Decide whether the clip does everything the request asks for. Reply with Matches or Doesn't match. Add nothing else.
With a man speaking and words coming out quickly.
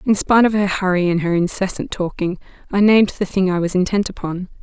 Doesn't match